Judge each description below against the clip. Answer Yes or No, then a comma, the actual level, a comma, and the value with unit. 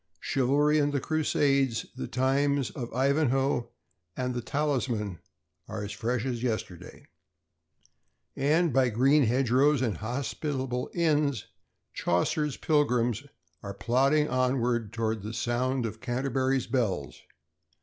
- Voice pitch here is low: Yes, low, 130 Hz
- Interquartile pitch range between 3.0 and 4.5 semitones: Yes, average, 3.3 semitones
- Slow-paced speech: Yes, slow, 115 wpm